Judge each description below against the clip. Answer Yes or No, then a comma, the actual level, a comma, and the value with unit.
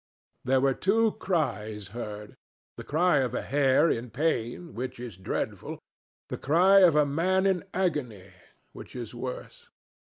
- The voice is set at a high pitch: No, low, 135 Hz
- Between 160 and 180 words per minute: No, average, 150 wpm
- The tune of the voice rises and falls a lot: Yes, wide, 6.7 semitones